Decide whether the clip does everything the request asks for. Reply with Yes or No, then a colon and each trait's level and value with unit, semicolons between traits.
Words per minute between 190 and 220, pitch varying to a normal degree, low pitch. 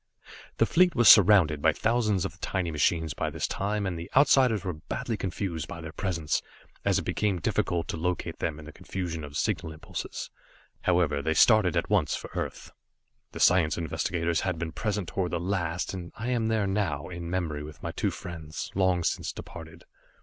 Yes: average, 195 wpm; average, 3.7 semitones; very low, 90 Hz